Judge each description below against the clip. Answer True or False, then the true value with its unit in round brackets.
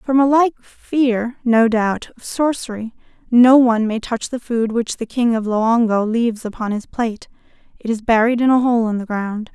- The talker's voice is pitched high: True (235 Hz)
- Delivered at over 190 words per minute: True (200 wpm)